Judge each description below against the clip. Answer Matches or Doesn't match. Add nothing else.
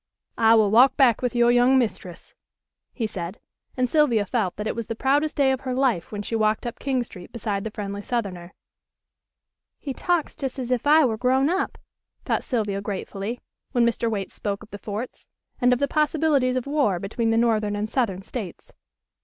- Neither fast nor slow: Matches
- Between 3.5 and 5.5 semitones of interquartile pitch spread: Matches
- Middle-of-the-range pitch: Doesn't match